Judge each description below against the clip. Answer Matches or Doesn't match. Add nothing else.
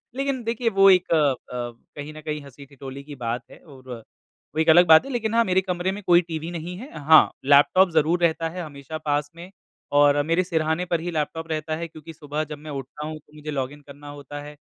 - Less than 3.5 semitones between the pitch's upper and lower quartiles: Matches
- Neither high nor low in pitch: Matches